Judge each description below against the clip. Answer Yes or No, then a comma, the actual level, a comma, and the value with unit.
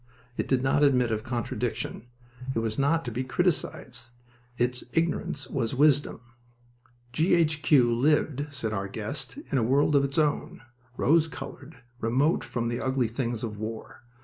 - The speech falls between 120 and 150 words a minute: No, average, 160 wpm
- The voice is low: Yes, low, 130 Hz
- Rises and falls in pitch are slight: No, average, 4.0 semitones